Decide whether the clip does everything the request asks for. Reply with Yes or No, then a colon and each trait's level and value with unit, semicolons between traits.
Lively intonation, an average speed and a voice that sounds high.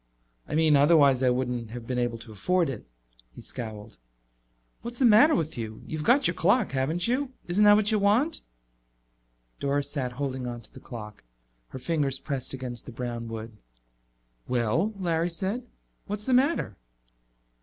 No: wide, 8.7 semitones; average, 165 wpm; medium, 140 Hz